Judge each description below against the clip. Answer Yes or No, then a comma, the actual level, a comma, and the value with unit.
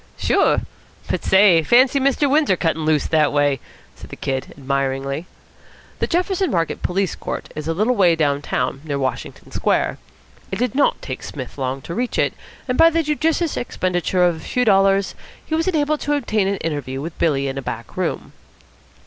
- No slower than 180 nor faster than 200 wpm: Yes, average, 185 wpm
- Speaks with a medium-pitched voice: Yes, medium, 175 Hz